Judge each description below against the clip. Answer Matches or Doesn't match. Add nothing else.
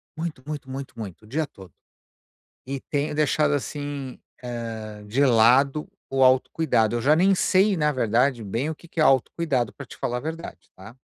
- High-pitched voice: Doesn't match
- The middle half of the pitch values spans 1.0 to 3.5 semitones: Doesn't match